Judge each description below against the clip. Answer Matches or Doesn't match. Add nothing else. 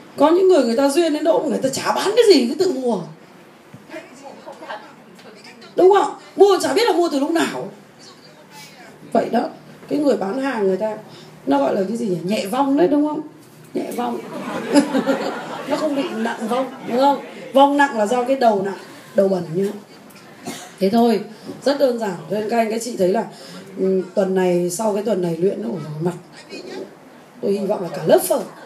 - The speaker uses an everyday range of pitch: Doesn't match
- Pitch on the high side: Matches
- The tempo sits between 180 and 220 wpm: Matches